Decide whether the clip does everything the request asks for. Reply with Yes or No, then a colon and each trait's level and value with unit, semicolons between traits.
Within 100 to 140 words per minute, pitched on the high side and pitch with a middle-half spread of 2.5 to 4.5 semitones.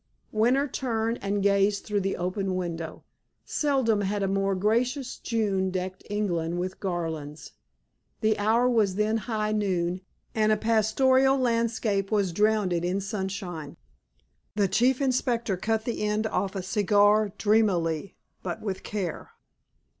Yes: slow, 135 wpm; high, 205 Hz; average, 3.0 semitones